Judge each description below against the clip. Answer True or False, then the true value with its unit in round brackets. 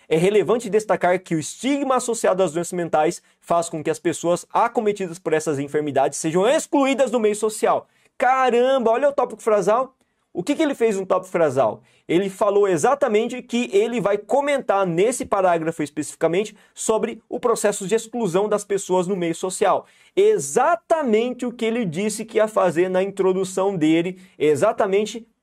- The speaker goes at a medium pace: True (165 wpm)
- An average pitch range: True (4.8 semitones)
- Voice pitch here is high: True (205 Hz)